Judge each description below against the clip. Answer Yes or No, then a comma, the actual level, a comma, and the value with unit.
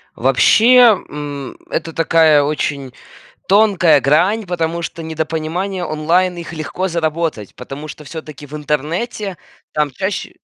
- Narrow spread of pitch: No, average, 3.3 semitones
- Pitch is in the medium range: Yes, medium, 160 Hz